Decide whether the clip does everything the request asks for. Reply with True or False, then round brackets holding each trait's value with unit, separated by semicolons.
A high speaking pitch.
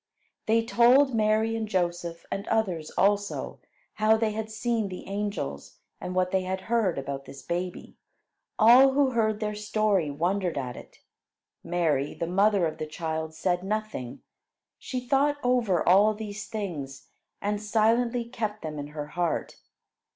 True (205 Hz)